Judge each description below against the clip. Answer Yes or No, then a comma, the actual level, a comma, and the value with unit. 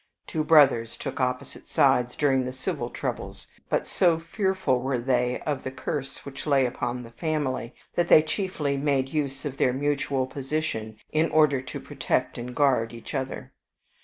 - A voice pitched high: No, low, 135 Hz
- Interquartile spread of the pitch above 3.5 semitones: No, average, 3.1 semitones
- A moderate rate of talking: Yes, average, 165 wpm